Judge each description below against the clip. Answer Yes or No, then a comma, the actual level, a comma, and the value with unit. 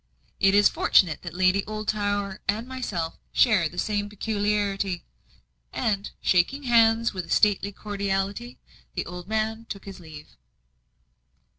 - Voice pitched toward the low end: No, high, 205 Hz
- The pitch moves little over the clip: Yes, narrow, 2.2 semitones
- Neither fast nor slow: No, slow, 130 wpm